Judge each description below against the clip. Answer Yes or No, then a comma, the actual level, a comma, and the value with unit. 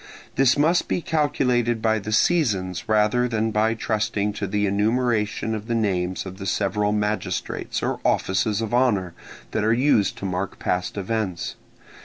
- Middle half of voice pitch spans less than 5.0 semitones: Yes, average, 3.0 semitones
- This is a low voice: Yes, low, 105 Hz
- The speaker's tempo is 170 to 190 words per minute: No, average, 160 wpm